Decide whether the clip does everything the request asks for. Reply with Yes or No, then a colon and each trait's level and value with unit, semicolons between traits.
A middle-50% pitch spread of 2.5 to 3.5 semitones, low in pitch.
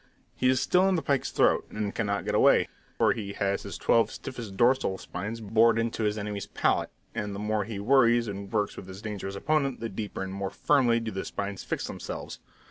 Yes: average, 3.0 semitones; low, 110 Hz